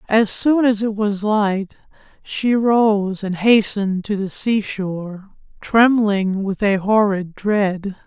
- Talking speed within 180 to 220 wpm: No, slow, 135 wpm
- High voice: Yes, high, 205 Hz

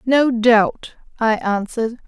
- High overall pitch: Yes, high, 235 Hz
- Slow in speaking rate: Yes, slow, 115 wpm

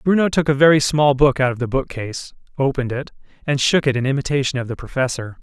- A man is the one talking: Yes, male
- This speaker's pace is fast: Yes, fast, 220 wpm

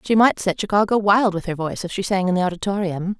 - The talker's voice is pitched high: Yes, high, 195 Hz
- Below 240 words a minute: No, fast, 265 wpm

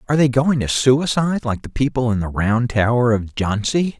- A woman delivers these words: No, male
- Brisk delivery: Yes, fast, 210 wpm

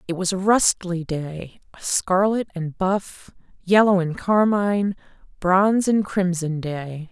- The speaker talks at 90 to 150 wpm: Yes, slow, 135 wpm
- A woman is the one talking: Yes, female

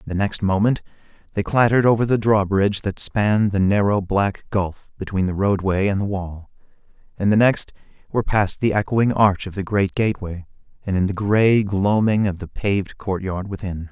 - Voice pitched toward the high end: No, low, 100 Hz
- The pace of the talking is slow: No, average, 185 wpm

